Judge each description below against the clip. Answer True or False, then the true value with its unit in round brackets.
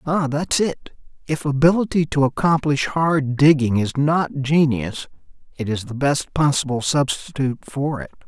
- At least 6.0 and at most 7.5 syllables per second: False (4.5 syllables/s)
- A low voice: False (145 Hz)